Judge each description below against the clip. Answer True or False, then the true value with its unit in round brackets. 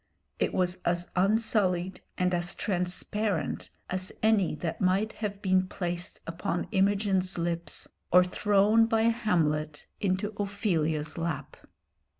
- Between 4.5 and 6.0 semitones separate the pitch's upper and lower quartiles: False (2.9 semitones)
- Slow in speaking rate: True (120 wpm)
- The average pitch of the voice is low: False (185 Hz)